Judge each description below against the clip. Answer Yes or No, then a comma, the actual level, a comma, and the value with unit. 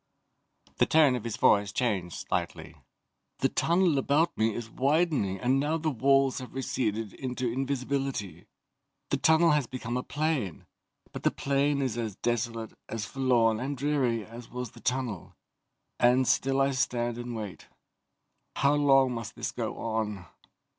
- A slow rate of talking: No, average, 155 wpm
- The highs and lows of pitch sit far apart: No, average, 3.4 semitones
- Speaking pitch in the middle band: No, low, 125 Hz